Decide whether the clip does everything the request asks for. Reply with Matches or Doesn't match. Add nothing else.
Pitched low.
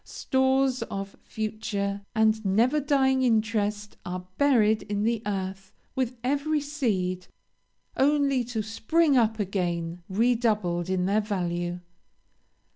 Doesn't match